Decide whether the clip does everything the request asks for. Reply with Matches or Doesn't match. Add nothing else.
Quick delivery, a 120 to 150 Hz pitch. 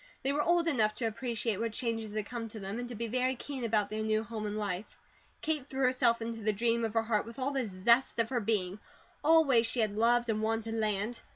Doesn't match